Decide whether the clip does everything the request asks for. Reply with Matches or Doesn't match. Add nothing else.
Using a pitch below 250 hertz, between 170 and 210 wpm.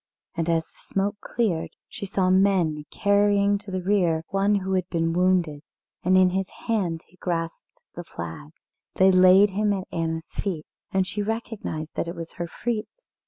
Matches